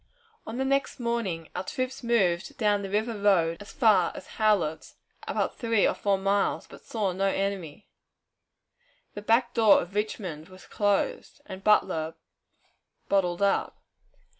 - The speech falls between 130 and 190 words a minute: Yes, average, 145 wpm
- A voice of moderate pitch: No, high, 200 Hz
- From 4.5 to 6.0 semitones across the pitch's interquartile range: No, average, 3.1 semitones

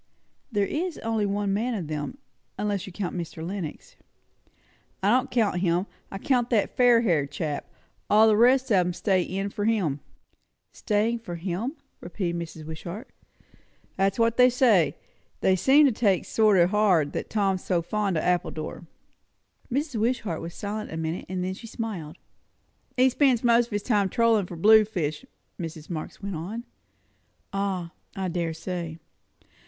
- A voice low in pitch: No, high, 195 Hz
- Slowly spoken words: No, average, 165 wpm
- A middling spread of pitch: Yes, average, 4.7 semitones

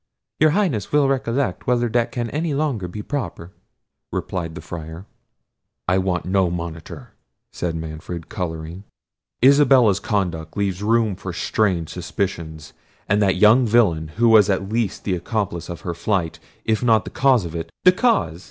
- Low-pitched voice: Yes, low, 100 Hz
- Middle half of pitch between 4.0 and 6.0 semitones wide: Yes, wide, 5.5 semitones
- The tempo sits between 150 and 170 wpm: Yes, average, 155 wpm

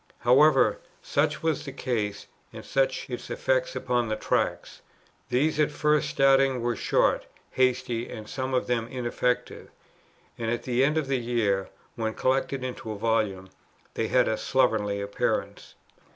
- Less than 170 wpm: Yes, average, 150 wpm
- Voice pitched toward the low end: Yes, low, 125 Hz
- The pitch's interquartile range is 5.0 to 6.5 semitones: No, average, 3.3 semitones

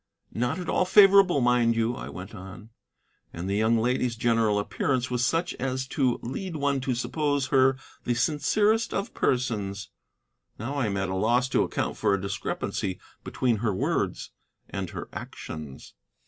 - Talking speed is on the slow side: No, average, 165 wpm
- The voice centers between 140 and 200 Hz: No, low, 125 Hz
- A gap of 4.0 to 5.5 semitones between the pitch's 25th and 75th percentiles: Yes, average, 4.8 semitones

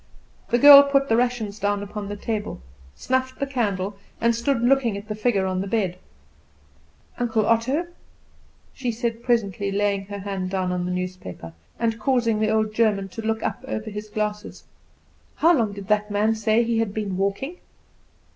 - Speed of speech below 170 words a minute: No, average, 175 wpm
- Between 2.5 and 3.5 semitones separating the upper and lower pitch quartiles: Yes, average, 2.8 semitones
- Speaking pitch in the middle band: No, high, 215 Hz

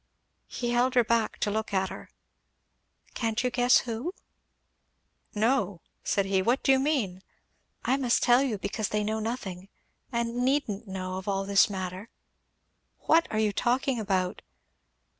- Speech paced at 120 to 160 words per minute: Yes, average, 155 wpm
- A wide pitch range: No, average, 4.0 semitones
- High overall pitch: Yes, high, 220 Hz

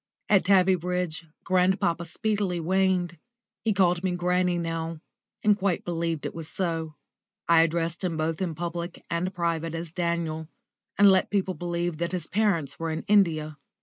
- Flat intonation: Yes, narrow, 2.1 semitones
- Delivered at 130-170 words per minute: Yes, average, 155 wpm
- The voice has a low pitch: No, medium, 175 Hz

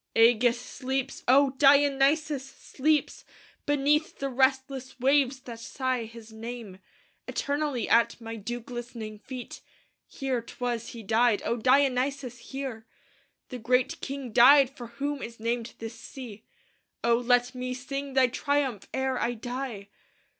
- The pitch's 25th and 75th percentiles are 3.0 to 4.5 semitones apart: No, narrow, 2.6 semitones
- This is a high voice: Yes, very high, 250 Hz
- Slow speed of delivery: Yes, slow, 130 wpm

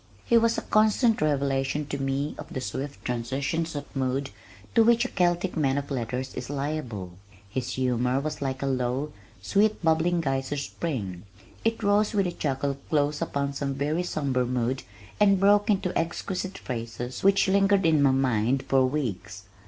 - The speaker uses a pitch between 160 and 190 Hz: No, medium, 140 Hz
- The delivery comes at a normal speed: Yes, average, 170 wpm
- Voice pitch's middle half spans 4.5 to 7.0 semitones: Yes, average, 5.1 semitones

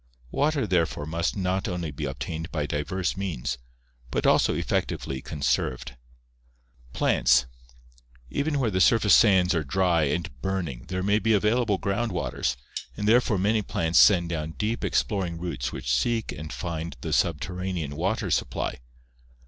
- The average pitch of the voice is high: No, very low, 90 Hz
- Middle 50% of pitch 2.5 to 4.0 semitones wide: No, wide, 5.4 semitones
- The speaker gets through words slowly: No, average, 150 wpm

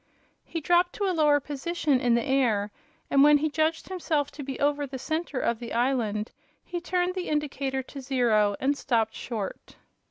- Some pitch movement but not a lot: Yes, average, 4.2 semitones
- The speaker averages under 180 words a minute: No, average, 185 wpm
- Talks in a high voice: Yes, very high, 280 Hz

